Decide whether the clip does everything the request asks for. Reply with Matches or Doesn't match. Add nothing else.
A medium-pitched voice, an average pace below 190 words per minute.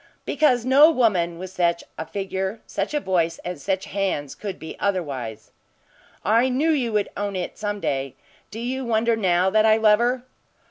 Doesn't match